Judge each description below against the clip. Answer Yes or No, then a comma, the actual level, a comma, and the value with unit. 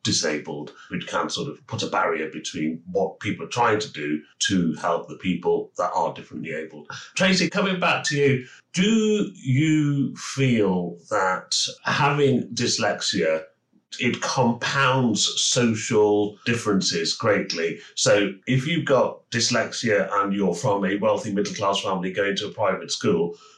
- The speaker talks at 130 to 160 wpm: Yes, average, 145 wpm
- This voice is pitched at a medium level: No, low, 115 Hz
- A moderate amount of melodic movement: No, wide, 7.3 semitones